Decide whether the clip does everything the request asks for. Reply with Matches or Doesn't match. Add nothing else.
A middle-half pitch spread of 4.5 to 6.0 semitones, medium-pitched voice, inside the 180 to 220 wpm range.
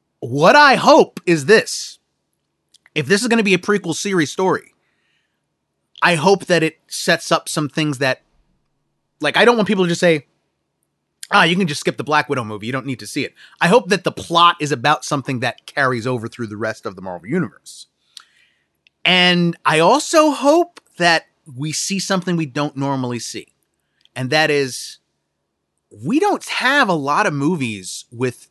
Matches